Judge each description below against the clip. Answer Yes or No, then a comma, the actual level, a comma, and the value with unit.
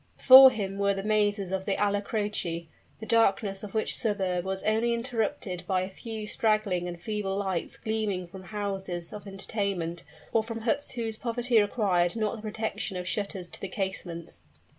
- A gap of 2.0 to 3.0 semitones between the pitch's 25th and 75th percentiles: Yes, narrow, 2.6 semitones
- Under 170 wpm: No, average, 175 wpm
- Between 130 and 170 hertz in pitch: No, high, 205 Hz